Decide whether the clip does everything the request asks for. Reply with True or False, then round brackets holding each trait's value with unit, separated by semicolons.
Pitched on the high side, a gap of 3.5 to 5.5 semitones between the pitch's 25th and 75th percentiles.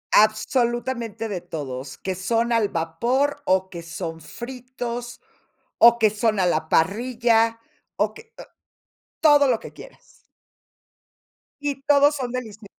True (230 Hz; 5.0 semitones)